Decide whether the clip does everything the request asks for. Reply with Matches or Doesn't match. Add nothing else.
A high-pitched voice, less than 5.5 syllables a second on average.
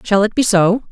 Matches